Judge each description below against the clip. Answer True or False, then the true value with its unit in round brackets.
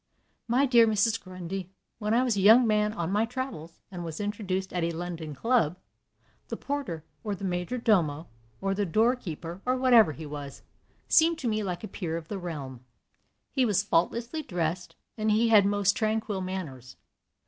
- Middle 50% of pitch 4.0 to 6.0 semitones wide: True (5.0 semitones)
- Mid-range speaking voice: False (195 Hz)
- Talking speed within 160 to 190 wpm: True (180 wpm)